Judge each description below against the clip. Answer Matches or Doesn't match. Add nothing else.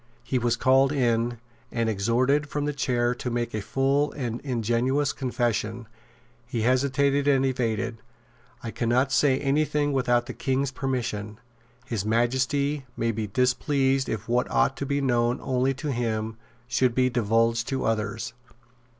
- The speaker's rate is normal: Matches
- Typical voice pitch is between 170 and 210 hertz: Doesn't match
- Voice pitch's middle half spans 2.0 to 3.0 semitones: Matches